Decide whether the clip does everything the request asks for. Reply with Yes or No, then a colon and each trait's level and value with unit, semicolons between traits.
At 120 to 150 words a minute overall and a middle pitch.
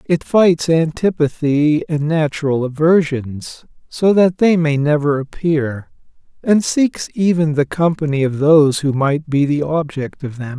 Yes: average, 145 wpm; medium, 155 Hz